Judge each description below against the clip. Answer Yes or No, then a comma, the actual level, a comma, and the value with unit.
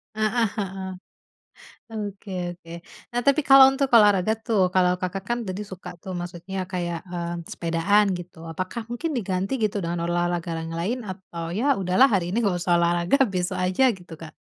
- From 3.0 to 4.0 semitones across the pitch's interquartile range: Yes, average, 3.5 semitones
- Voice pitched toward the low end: No, medium, 185 Hz